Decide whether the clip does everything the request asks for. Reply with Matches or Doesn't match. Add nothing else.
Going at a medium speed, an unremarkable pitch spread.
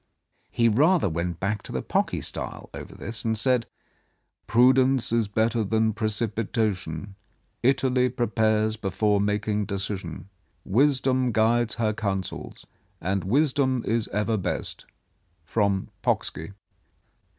Doesn't match